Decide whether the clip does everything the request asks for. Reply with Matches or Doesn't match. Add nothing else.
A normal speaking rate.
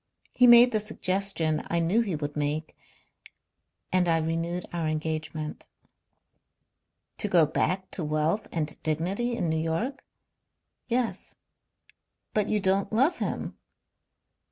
Doesn't match